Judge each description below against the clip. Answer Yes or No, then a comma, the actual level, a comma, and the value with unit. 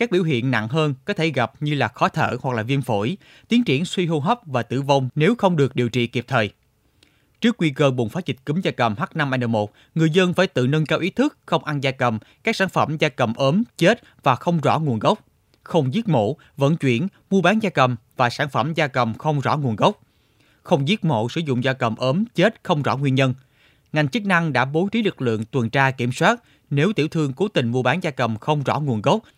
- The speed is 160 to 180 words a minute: No, average, 245 wpm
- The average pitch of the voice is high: No, medium, 145 Hz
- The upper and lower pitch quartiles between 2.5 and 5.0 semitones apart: No, wide, 5.6 semitones